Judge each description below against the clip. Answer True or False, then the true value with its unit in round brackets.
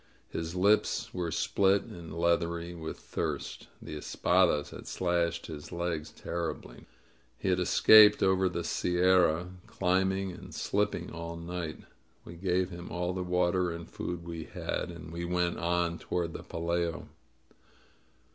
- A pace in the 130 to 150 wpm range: True (140 wpm)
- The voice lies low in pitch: True (85 Hz)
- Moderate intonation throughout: False (1.4 semitones)